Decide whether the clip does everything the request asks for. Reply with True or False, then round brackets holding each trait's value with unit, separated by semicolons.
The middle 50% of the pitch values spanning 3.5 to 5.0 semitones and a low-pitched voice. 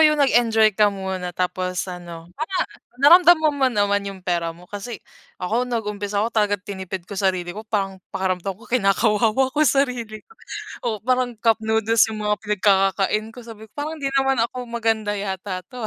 False (4.0 semitones; 210 Hz)